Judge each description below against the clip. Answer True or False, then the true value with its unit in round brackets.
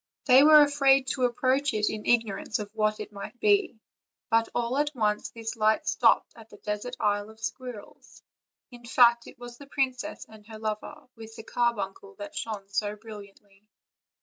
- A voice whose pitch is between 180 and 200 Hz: False (225 Hz)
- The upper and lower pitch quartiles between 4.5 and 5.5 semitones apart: False (3.3 semitones)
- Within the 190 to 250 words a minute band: False (175 wpm)